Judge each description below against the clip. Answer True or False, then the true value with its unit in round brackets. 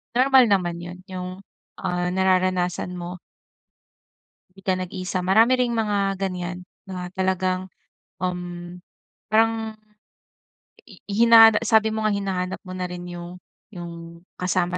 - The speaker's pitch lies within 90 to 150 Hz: False (185 Hz)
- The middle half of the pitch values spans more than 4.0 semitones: False (2.6 semitones)